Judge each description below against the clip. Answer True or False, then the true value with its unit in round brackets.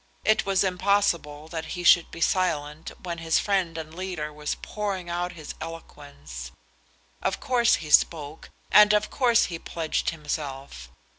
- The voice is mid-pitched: True (165 Hz)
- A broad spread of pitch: False (3.9 semitones)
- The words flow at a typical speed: True (150 wpm)